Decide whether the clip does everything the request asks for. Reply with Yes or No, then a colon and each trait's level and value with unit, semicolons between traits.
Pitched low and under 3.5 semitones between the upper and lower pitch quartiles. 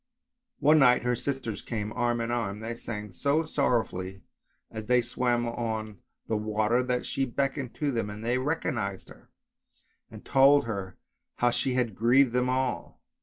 Yes: low, 120 Hz; average, 3.1 semitones